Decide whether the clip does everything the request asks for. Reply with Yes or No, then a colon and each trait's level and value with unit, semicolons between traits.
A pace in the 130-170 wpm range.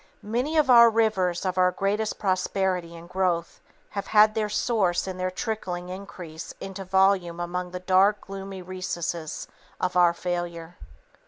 Yes: average, 150 wpm